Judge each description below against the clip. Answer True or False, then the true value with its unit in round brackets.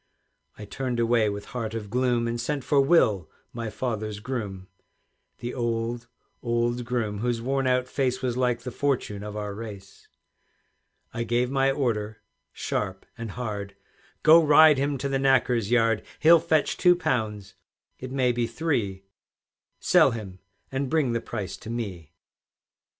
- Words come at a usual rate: True (155 wpm)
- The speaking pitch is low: True (120 Hz)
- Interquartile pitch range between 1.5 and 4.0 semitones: True (3.6 semitones)